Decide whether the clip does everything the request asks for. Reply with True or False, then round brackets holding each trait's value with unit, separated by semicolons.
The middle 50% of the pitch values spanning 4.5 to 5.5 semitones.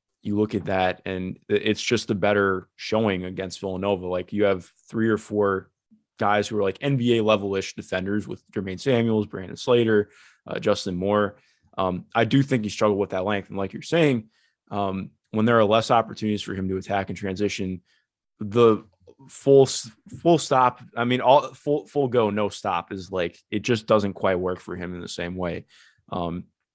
False (3.2 semitones)